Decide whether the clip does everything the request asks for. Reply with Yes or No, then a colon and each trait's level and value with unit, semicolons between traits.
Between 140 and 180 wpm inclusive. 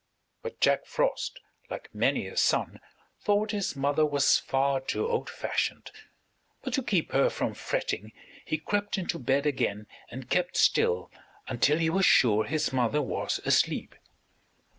Yes: average, 150 wpm